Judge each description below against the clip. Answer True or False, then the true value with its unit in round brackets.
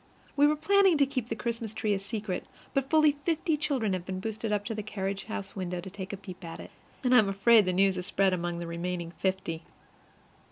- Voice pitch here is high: True (200 Hz)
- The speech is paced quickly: True (235 wpm)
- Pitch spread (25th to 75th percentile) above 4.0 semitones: True (4.9 semitones)